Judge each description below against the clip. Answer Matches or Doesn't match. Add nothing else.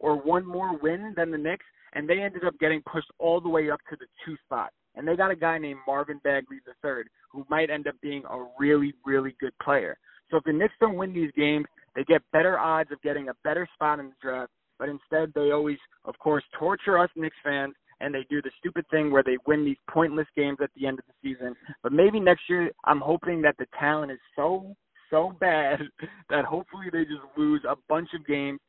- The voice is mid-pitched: Matches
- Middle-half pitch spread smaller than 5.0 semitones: Matches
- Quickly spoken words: Matches